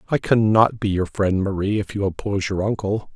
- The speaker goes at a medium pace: No, fast, 210 wpm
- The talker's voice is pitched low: Yes, low, 100 Hz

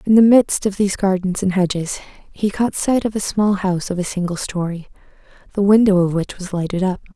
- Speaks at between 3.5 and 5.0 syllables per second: No, 5.7 syllables/s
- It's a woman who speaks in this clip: Yes, female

